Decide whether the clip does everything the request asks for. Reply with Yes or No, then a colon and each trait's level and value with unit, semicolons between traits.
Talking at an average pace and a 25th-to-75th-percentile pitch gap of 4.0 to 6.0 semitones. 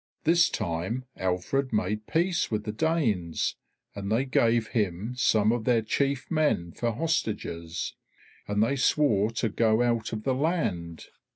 Yes: average, 150 wpm; average, 5.0 semitones